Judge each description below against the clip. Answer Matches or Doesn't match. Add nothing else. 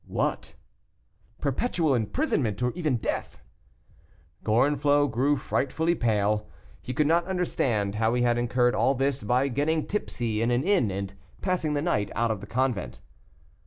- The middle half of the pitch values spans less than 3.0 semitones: Doesn't match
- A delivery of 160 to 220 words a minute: Doesn't match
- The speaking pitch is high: Doesn't match